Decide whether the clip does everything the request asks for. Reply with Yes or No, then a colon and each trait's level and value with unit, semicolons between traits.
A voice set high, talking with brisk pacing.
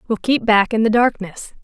Yes: high, 220 Hz; fast, 220 wpm